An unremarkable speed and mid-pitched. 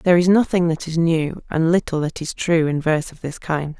No: fast, 255 wpm; medium, 165 Hz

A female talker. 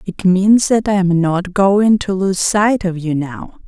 Yes: female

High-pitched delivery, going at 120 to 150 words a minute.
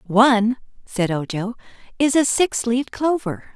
Yes: high, 235 Hz; slow, 135 wpm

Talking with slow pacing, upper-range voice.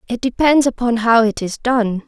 No: average, 200 wpm; high, 235 Hz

